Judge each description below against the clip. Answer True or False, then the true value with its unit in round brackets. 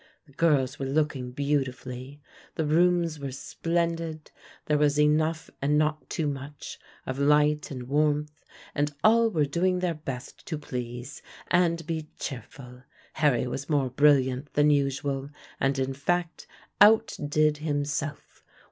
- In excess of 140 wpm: False (135 wpm)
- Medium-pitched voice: True (150 Hz)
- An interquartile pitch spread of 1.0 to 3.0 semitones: True (2.5 semitones)